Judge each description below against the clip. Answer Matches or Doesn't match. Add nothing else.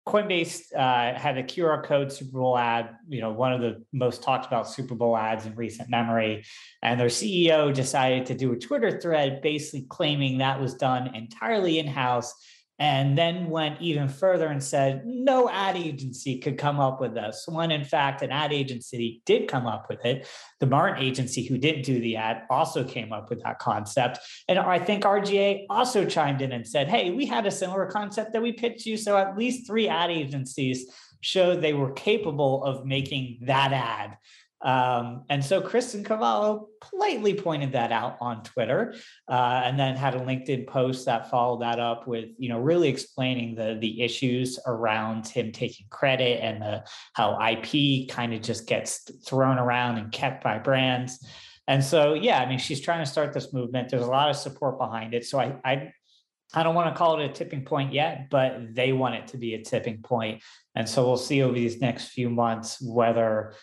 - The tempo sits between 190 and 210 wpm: Matches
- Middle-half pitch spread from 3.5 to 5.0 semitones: Matches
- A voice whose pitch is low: Matches